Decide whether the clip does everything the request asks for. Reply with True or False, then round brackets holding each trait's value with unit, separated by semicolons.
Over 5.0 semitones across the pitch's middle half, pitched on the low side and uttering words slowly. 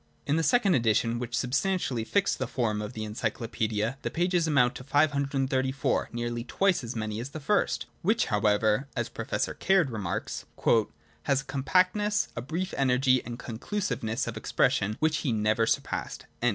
False (5.6 semitones; 130 Hz; 165 wpm)